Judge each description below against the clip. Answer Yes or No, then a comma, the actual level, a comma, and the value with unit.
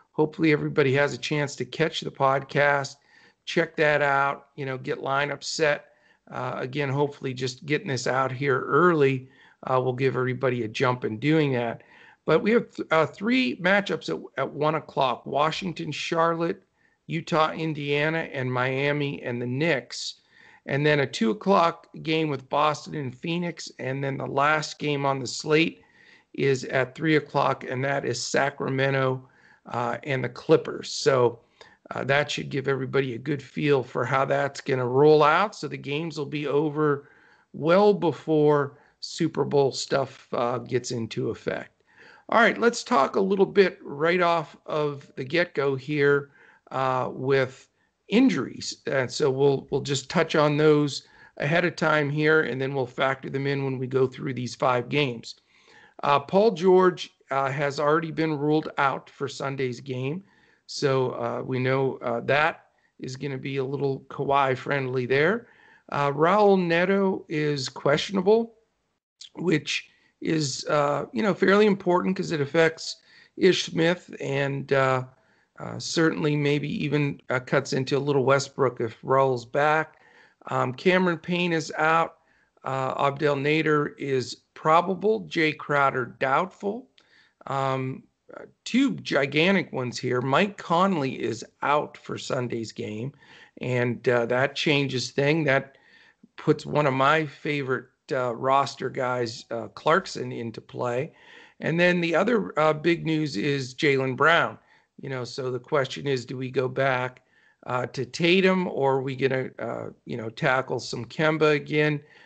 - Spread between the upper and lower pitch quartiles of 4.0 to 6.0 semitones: No, average, 3.1 semitones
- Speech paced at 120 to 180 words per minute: Yes, average, 155 wpm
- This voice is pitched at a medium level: Yes, medium, 145 Hz